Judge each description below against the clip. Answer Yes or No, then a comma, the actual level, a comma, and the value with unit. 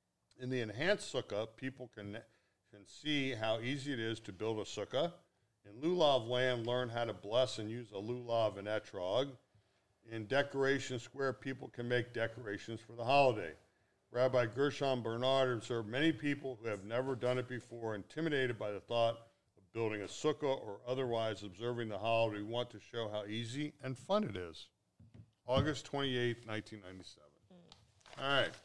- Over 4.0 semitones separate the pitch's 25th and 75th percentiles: No, average, 3.3 semitones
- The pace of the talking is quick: No, average, 165 wpm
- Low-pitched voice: Yes, low, 120 Hz